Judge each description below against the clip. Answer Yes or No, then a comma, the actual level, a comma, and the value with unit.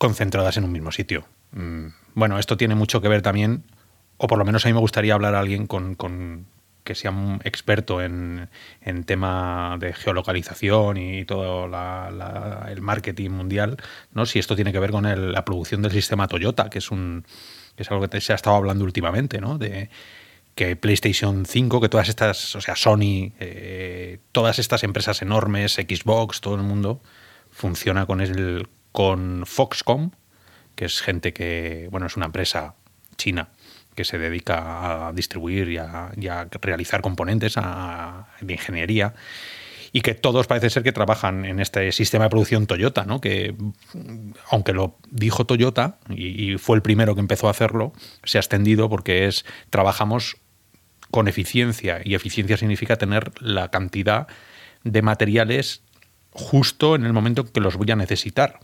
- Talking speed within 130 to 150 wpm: No, average, 170 wpm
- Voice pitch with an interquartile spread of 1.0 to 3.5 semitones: Yes, average, 2.9 semitones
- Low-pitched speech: Yes, low, 100 Hz